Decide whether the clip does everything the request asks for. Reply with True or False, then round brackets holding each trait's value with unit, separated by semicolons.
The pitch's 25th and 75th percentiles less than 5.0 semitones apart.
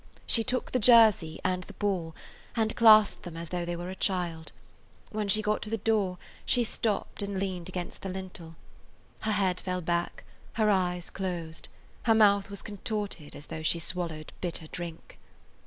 True (3.5 semitones)